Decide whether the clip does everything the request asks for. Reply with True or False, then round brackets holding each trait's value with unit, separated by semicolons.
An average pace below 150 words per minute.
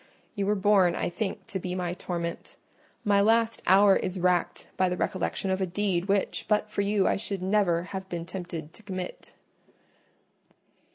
False (175 wpm)